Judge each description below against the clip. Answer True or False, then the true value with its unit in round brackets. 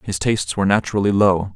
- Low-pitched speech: True (100 Hz)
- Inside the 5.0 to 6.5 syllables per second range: False (6.9 syllables/s)